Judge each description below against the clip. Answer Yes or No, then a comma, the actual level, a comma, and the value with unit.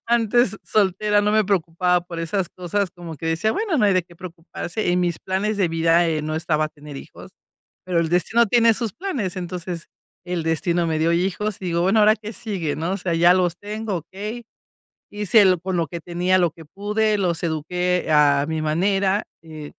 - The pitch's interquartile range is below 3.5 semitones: No, average, 3.8 semitones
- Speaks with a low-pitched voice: No, medium, 180 Hz